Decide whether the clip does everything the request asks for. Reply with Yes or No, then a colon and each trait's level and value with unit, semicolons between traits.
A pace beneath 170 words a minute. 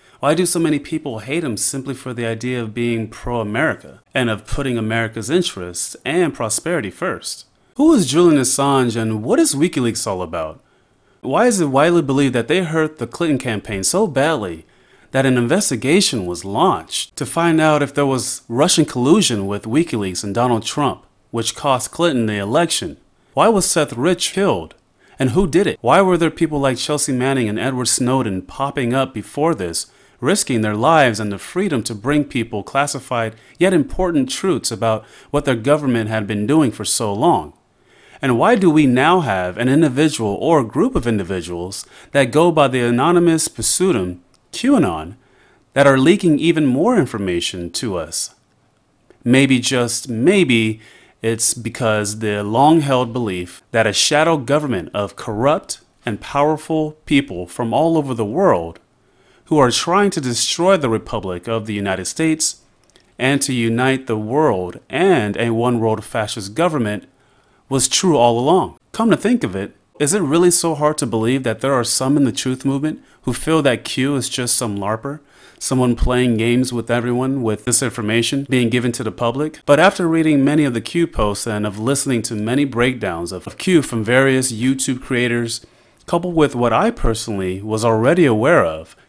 No: average, 175 wpm